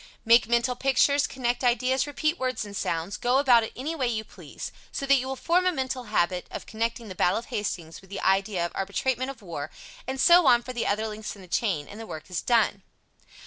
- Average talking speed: No, fast, 230 wpm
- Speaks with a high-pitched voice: Yes, high, 235 Hz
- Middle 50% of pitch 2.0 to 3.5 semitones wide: No, average, 4.7 semitones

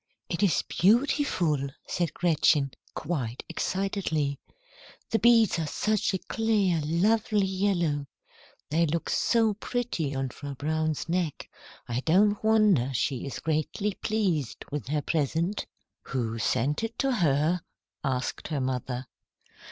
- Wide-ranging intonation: Yes, wide, 6.3 semitones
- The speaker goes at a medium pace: No, slow, 125 wpm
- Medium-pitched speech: Yes, medium, 165 Hz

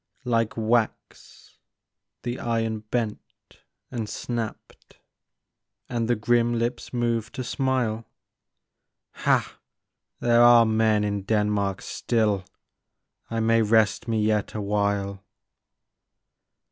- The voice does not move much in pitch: Yes, narrow, 2.0 semitones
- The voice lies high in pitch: No, low, 115 Hz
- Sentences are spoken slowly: Yes, slow, 105 wpm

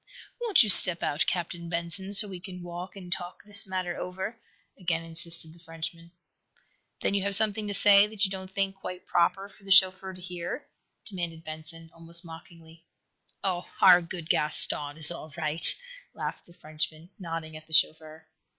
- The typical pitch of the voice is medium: Yes, medium, 175 Hz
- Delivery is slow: No, average, 175 wpm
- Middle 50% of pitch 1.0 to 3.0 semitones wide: Yes, narrow, 2.6 semitones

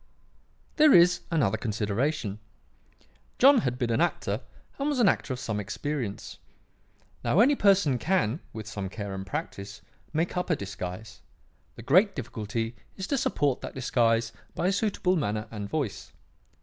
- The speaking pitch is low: Yes, low, 125 Hz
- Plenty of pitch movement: Yes, wide, 8.9 semitones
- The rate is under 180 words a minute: Yes, average, 155 wpm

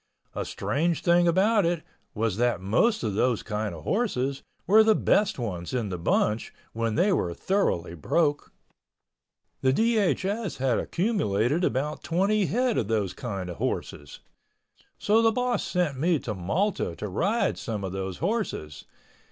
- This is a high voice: No, medium, 140 Hz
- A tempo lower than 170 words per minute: Yes, average, 155 wpm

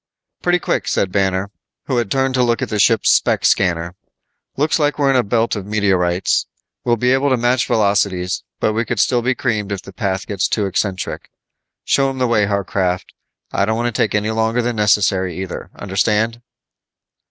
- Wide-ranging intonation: No, average, 3.8 semitones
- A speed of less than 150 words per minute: No, average, 195 wpm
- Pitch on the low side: Yes, low, 105 Hz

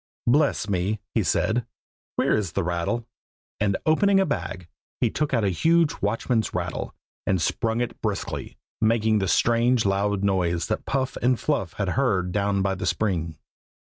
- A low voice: Yes, low, 105 Hz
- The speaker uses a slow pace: No, average, 165 wpm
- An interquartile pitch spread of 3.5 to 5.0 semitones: Yes, average, 4.4 semitones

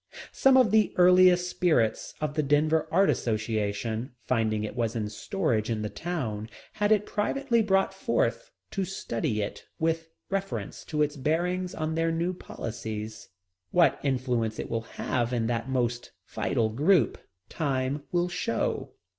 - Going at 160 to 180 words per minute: No, average, 150 wpm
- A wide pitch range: Yes, wide, 7.8 semitones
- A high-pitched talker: No, medium, 145 Hz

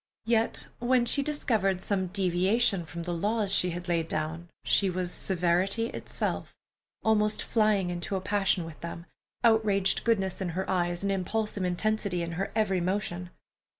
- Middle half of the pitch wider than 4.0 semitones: No, average, 3.4 semitones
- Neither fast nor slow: Yes, average, 155 wpm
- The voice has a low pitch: No, high, 190 Hz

